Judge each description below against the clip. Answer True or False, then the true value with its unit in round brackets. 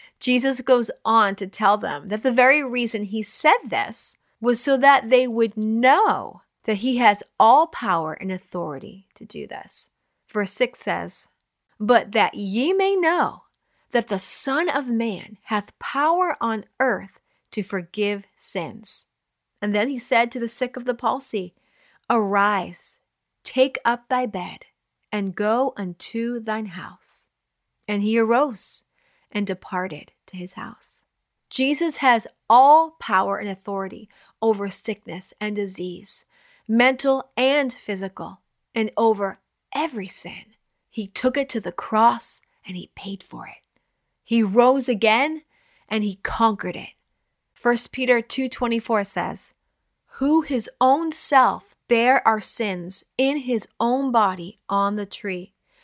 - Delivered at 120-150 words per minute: True (140 wpm)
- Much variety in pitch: False (4.2 semitones)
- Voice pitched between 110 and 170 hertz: False (225 Hz)